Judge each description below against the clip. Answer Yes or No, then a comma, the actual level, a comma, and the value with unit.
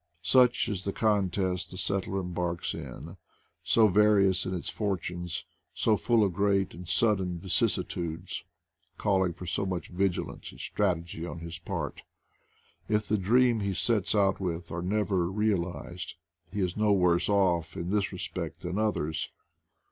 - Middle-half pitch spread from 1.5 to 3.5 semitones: Yes, average, 2.9 semitones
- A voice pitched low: Yes, very low, 95 Hz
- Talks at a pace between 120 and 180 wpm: Yes, average, 155 wpm